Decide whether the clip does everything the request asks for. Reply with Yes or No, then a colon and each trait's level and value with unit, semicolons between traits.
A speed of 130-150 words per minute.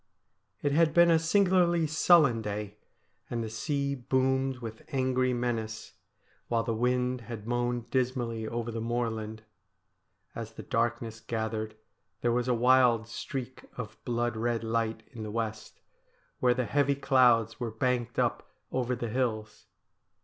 Yes: average, 145 wpm